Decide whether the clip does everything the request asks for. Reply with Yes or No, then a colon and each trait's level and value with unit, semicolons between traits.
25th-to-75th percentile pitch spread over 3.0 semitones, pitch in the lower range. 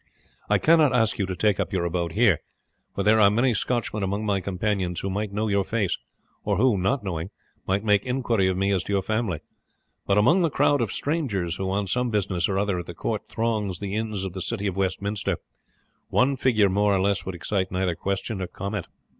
No: average, 2.7 semitones; low, 100 Hz